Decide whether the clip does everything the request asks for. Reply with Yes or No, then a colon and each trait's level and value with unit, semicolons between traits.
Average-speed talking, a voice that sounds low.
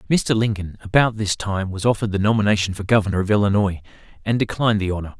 Yes: average, 195 wpm; low, 105 Hz